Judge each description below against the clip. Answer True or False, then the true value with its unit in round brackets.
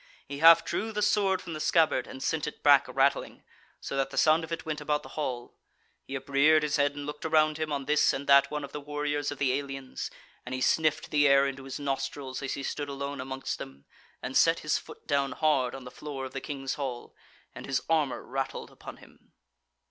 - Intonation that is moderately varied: False (2.2 semitones)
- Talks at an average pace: False (225 wpm)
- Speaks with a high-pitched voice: False (140 Hz)